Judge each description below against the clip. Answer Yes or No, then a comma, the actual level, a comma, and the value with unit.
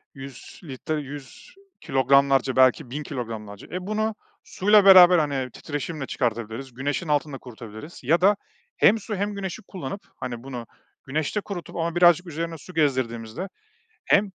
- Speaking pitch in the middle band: Yes, medium, 145 Hz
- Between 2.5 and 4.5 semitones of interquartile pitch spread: No, wide, 5.5 semitones